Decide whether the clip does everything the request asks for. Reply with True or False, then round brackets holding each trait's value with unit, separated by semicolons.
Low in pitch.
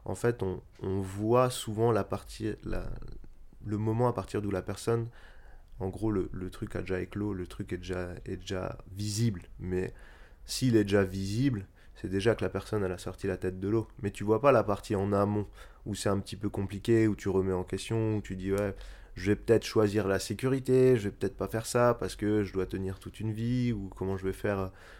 True (100 Hz)